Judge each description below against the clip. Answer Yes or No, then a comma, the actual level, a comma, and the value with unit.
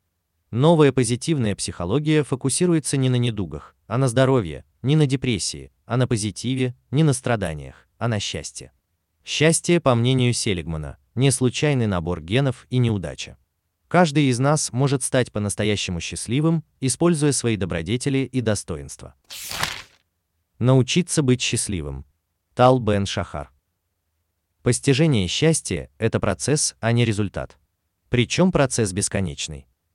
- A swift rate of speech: No, average, 120 wpm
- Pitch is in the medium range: No, low, 115 Hz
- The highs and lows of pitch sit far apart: Yes, wide, 7.4 semitones